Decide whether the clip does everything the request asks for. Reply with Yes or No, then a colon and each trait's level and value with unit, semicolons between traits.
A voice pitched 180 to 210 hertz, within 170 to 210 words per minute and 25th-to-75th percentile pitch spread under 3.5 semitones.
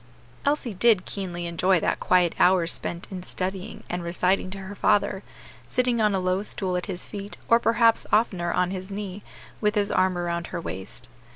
Yes: high, 190 Hz; average, 185 wpm; narrow, 2.5 semitones